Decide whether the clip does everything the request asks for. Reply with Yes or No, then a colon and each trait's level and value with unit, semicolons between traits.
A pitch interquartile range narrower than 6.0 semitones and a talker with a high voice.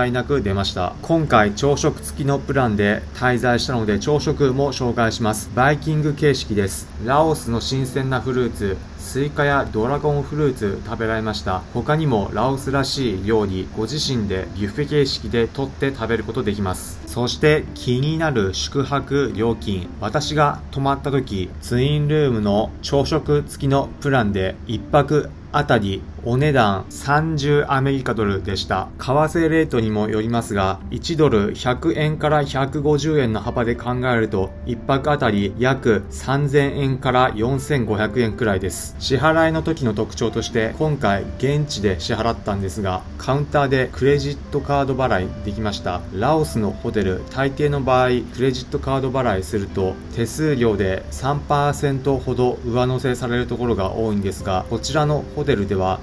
No: average, 5.3 semitones; low, 125 Hz